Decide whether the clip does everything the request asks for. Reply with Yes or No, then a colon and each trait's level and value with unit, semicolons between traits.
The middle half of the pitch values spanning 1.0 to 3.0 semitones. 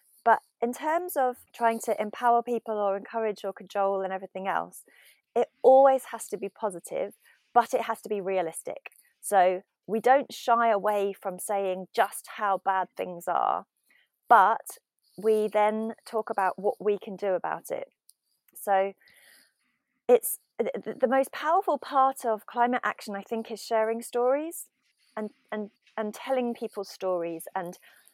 No: average, 3.7 semitones